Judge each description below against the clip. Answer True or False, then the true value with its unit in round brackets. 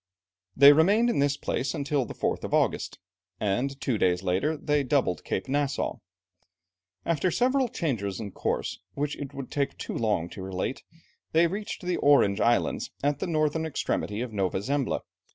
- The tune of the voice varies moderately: False (6.6 semitones)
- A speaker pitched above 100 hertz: True (140 Hz)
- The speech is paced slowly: False (170 wpm)